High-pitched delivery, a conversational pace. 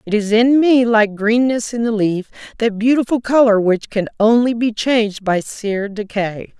Yes: high, 220 Hz; average, 175 wpm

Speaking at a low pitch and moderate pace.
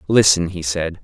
Yes: very low, 90 Hz; average, 175 wpm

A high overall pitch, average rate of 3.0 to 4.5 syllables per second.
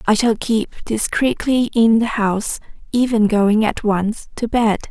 Yes: high, 220 Hz; 4.2 syllables/s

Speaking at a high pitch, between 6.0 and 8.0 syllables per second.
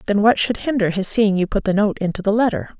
Yes: high, 205 Hz; 6.2 syllables/s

